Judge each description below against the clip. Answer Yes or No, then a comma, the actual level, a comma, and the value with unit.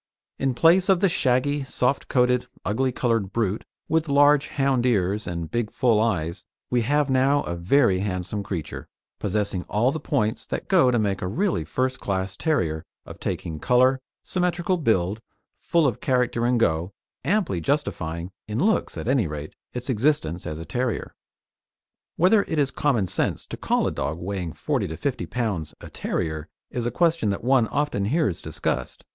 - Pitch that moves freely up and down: Yes, wide, 7.0 semitones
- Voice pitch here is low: Yes, low, 120 Hz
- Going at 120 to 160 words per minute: No, average, 175 wpm